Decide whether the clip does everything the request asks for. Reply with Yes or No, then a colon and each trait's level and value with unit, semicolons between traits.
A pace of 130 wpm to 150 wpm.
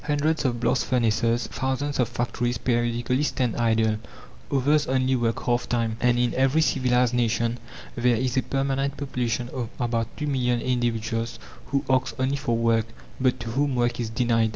No: average, 170 wpm